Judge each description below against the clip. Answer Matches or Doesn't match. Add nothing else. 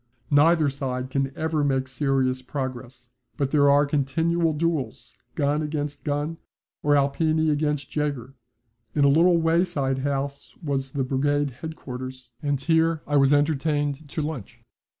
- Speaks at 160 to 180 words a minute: Doesn't match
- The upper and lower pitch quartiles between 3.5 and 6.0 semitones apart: Doesn't match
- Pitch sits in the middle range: Matches